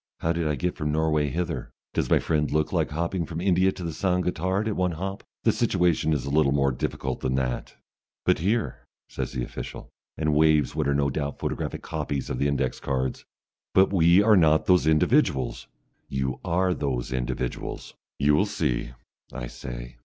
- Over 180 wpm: Yes, average, 190 wpm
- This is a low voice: Yes, very low, 75 Hz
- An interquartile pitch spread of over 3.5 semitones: Yes, average, 4.5 semitones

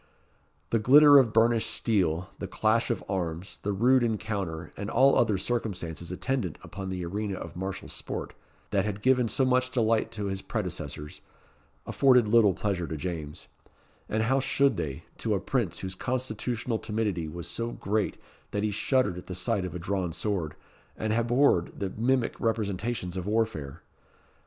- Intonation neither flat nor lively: Yes, average, 4.4 semitones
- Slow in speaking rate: No, average, 165 wpm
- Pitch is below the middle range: Yes, low, 105 Hz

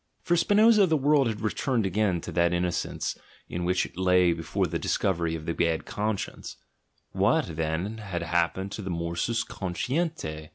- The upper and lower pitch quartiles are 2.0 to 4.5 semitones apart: No, average, 4.9 semitones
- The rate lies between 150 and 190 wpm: Yes, average, 170 wpm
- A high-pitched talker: No, very low, 90 Hz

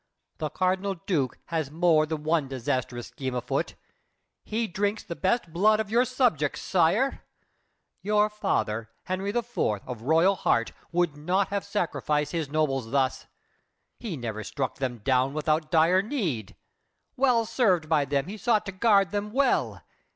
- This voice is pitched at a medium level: Yes, medium, 165 Hz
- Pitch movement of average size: No, wide, 6.6 semitones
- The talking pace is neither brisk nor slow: Yes, average, 150 wpm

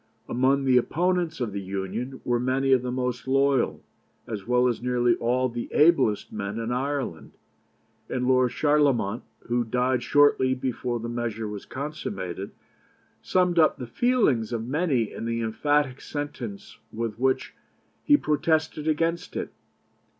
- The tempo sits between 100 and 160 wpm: Yes, average, 145 wpm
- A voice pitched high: No, low, 125 Hz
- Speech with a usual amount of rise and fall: Yes, average, 3.8 semitones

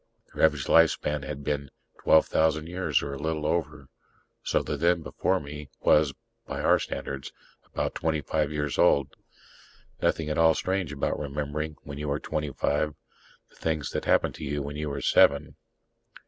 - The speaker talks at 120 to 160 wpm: No, average, 170 wpm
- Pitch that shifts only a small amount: Yes, narrow, 1.6 semitones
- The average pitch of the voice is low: Yes, very low, 75 Hz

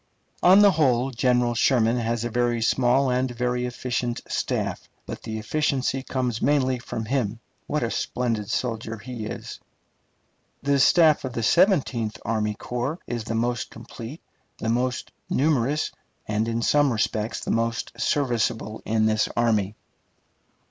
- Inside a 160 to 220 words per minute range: No, average, 145 wpm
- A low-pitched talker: Yes, low, 120 Hz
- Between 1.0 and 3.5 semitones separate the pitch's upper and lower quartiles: Yes, narrow, 2.6 semitones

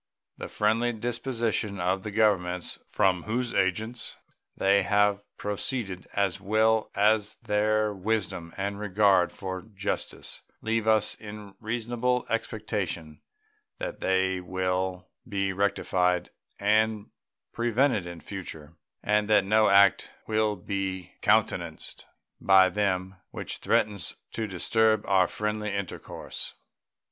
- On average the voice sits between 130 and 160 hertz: No, low, 100 Hz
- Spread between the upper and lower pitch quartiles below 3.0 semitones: Yes, narrow, 2.5 semitones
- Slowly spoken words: Yes, slow, 115 wpm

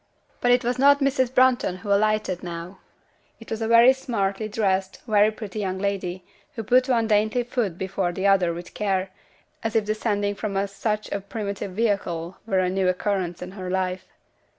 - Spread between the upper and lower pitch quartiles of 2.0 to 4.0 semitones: Yes, average, 3.0 semitones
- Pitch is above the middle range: Yes, high, 200 Hz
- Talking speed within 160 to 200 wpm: Yes, average, 180 wpm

